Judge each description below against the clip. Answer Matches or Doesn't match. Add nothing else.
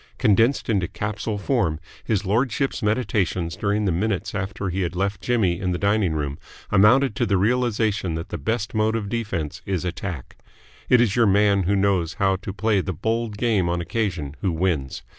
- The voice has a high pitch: Doesn't match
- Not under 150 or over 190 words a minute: Matches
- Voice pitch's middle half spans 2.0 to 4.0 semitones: Matches